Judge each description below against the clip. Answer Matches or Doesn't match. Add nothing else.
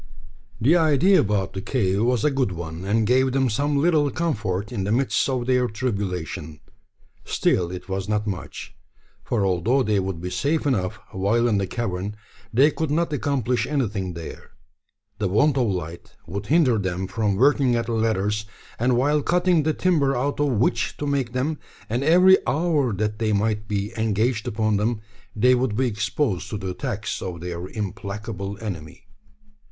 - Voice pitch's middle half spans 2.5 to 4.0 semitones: Doesn't match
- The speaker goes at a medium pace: Matches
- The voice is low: Matches